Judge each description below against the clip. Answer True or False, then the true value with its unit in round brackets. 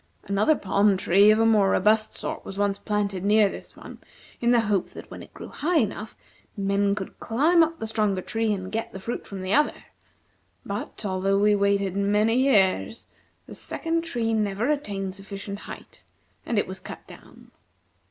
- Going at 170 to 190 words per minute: True (180 wpm)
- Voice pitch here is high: True (205 Hz)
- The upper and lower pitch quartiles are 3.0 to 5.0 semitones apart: False (2.4 semitones)